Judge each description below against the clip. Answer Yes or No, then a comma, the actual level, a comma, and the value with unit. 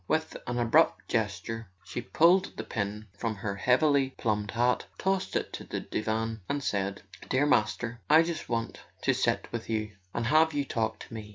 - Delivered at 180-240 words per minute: Yes, average, 185 wpm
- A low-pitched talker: Yes, low, 115 Hz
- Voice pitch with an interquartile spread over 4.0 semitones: Yes, average, 4.7 semitones